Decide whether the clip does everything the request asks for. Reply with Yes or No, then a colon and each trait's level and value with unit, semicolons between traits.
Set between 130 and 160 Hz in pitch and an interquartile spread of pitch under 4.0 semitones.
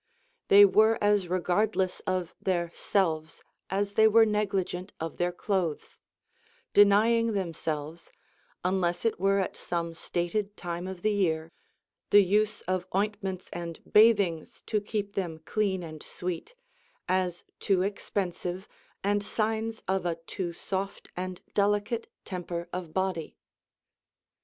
No: high, 190 Hz; average, 2.8 semitones